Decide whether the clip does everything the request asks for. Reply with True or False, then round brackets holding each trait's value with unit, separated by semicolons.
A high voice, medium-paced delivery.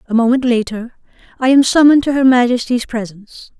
True (245 Hz; 165 wpm)